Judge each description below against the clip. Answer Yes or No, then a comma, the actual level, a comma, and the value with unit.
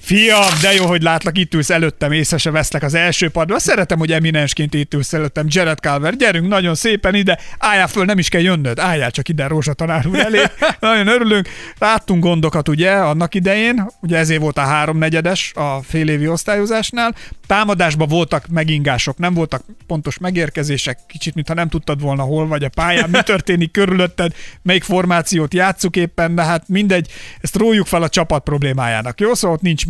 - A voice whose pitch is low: No, medium, 170 Hz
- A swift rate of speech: Yes, fast, 180 wpm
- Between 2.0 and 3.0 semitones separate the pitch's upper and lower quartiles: No, average, 3.4 semitones